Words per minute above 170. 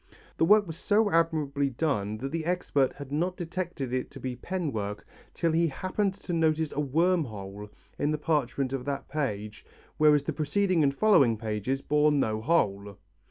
Yes: average, 180 wpm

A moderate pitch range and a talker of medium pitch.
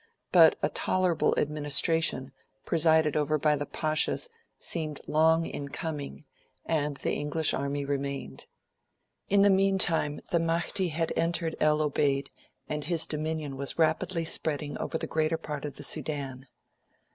No: narrow, 2.2 semitones; medium, 155 Hz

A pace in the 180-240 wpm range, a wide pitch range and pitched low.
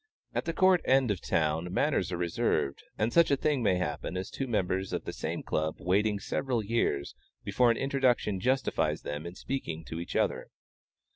Yes: average, 195 wpm; wide, 7.4 semitones; low, 105 Hz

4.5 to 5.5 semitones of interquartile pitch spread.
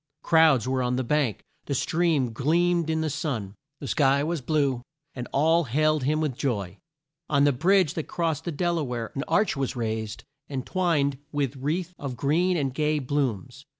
No: average, 3.8 semitones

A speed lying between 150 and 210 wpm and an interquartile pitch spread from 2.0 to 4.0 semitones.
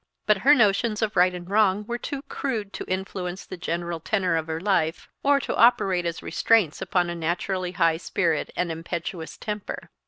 Yes: average, 180 wpm; average, 3.6 semitones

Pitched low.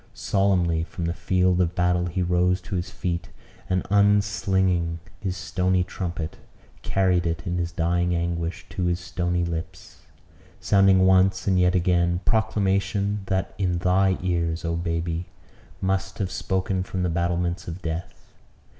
Yes: very low, 90 Hz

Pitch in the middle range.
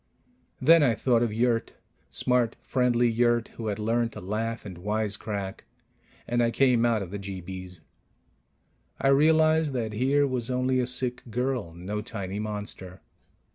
No: low, 115 Hz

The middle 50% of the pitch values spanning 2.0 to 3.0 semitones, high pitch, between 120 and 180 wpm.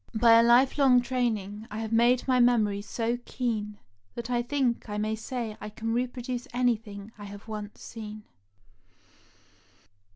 Yes: narrow, 2.6 semitones; high, 230 Hz; average, 155 wpm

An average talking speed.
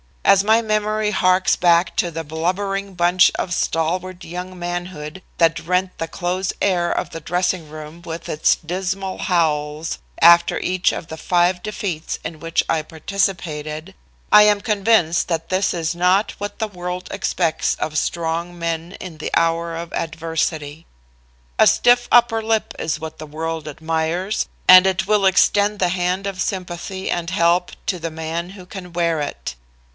Yes: average, 160 wpm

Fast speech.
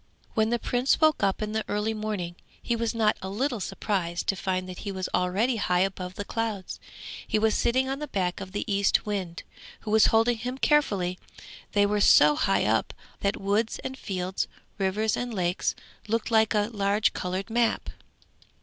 No: average, 185 wpm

